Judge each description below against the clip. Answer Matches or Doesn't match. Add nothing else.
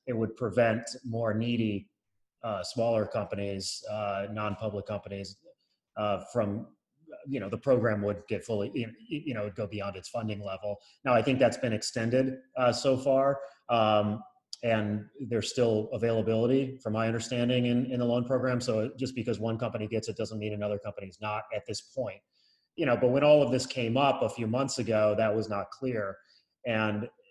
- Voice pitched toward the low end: Matches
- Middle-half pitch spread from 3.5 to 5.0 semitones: Doesn't match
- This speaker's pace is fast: Doesn't match